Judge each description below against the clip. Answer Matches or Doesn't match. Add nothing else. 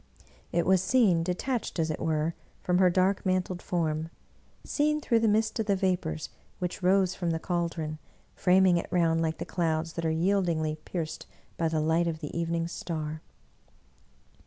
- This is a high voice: Doesn't match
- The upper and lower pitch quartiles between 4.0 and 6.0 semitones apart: Doesn't match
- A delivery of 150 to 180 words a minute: Matches